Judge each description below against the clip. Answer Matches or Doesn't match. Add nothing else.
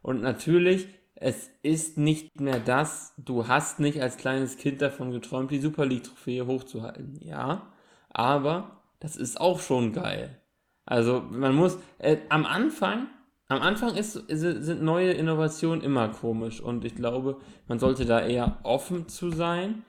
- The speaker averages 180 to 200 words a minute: Doesn't match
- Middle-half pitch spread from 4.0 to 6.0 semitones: Matches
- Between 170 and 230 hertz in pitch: Doesn't match